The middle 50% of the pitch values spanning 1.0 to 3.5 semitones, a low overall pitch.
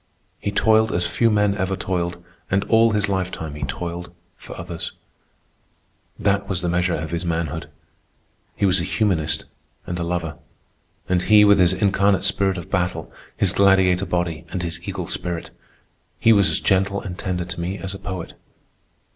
Yes: narrow, 2.5 semitones; very low, 90 Hz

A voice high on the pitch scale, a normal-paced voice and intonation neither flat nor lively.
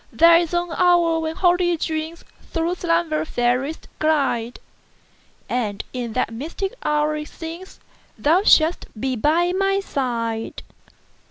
No: very high, 320 Hz; slow, 110 wpm; average, 4.7 semitones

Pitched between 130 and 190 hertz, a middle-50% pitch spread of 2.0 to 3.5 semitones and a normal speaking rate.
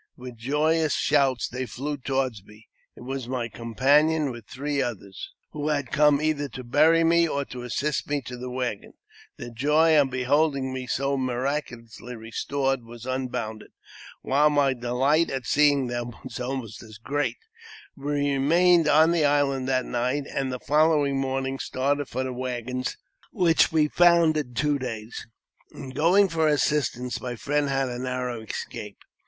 Yes: low, 135 Hz; average, 3.0 semitones; average, 165 wpm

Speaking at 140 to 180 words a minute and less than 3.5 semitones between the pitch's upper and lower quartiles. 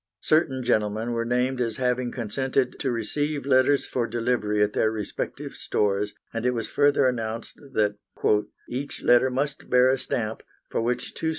Yes: average, 170 wpm; average, 2.8 semitones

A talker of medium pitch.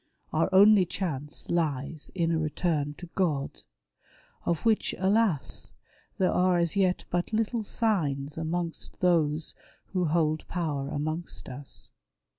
Yes: medium, 170 Hz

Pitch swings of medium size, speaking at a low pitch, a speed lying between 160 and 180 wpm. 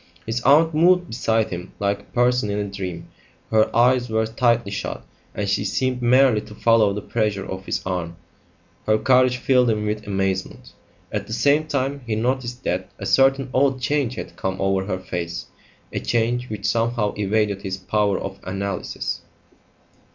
Yes: average, 4.1 semitones; low, 110 Hz; average, 175 wpm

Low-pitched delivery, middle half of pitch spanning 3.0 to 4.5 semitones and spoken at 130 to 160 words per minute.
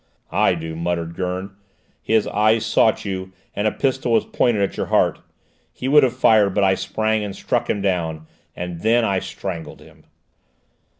No: low, 100 Hz; average, 3.6 semitones; average, 175 wpm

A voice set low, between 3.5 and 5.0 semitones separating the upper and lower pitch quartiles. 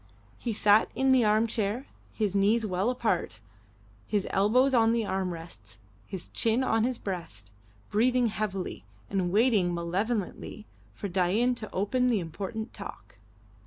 No: high, 210 Hz; average, 3.9 semitones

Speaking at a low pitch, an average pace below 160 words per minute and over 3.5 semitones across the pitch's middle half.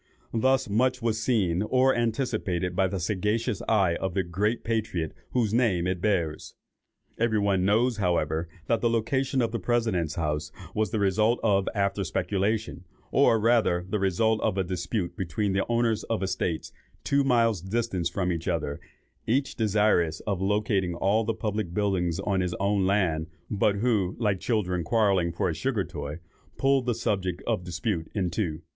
No: low, 100 Hz; average, 170 wpm; average, 4.1 semitones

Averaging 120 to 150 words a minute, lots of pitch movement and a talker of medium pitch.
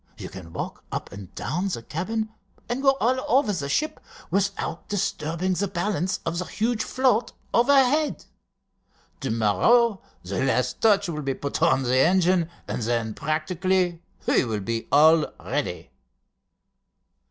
Yes: average, 145 wpm; wide, 8.1 semitones; medium, 175 Hz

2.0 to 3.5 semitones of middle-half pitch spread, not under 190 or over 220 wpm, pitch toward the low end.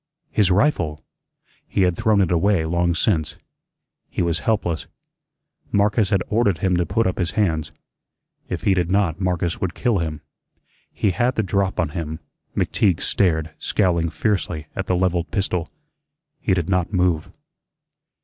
No: average, 3.1 semitones; average, 155 wpm; very low, 90 Hz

